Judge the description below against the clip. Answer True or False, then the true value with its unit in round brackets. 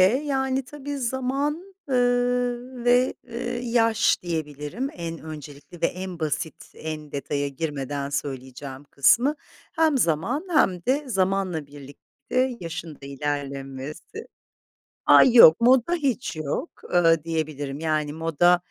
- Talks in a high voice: False (175 Hz)